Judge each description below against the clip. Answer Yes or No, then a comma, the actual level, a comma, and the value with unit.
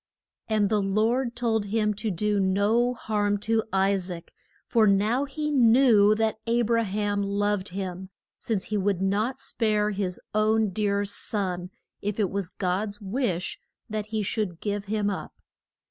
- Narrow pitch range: Yes, narrow, 2.1 semitones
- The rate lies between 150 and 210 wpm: Yes, average, 160 wpm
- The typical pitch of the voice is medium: No, high, 210 Hz